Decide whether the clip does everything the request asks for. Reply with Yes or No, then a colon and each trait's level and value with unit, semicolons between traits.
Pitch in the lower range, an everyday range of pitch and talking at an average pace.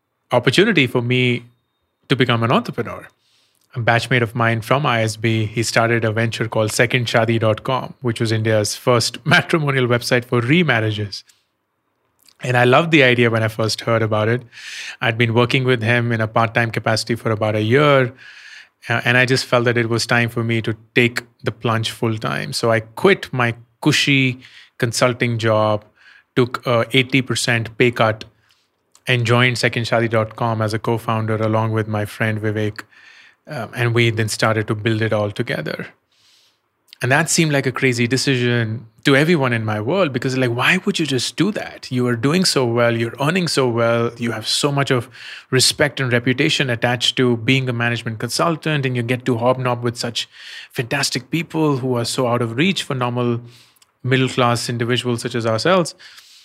No: low, 120 Hz; narrow, 2.1 semitones; average, 180 wpm